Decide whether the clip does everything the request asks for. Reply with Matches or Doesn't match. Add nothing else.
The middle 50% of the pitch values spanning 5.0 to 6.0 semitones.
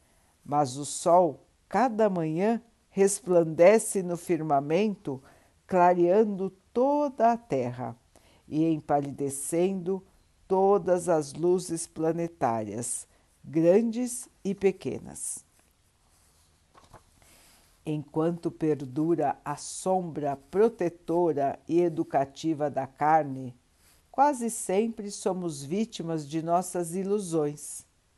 Matches